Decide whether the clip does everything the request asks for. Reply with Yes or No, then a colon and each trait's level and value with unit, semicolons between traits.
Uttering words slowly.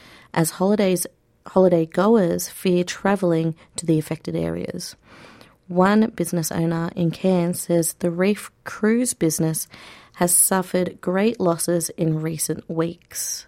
Yes: slow, 120 wpm